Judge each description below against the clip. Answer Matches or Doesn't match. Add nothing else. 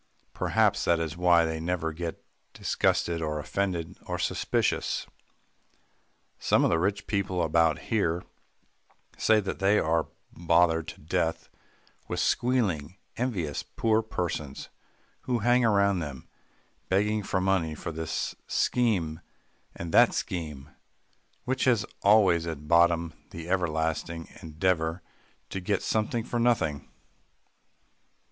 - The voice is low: Matches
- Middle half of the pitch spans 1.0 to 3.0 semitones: Doesn't match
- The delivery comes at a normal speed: Doesn't match